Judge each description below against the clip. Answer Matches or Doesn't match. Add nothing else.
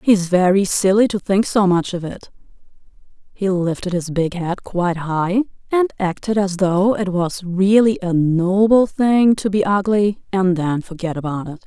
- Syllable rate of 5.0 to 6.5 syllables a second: Doesn't match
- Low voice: Doesn't match